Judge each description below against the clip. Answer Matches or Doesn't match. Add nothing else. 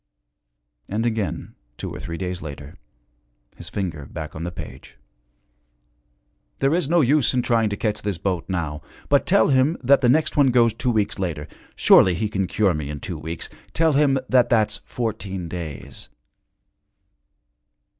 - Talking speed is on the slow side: Doesn't match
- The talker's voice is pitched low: Matches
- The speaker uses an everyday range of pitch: Doesn't match